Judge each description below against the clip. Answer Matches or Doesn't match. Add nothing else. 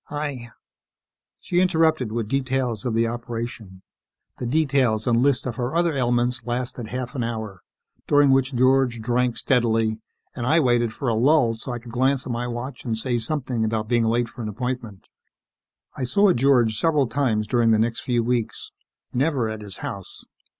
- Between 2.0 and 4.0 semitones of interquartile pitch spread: Matches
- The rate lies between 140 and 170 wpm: Doesn't match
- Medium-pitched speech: Doesn't match